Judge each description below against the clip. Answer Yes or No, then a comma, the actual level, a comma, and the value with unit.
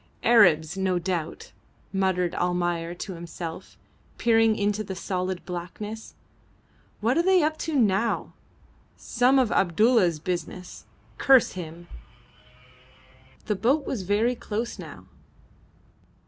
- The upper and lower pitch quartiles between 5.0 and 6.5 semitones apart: No, average, 4.6 semitones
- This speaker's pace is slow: Yes, slow, 110 wpm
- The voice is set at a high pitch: Yes, high, 195 Hz